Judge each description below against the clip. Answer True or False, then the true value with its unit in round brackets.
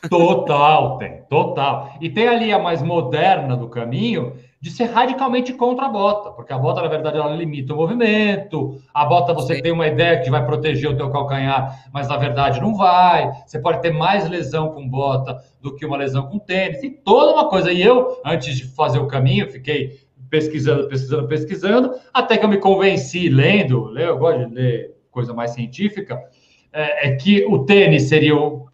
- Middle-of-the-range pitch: True (155 Hz)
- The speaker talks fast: True (190 wpm)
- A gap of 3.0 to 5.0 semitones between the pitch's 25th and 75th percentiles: False (5.5 semitones)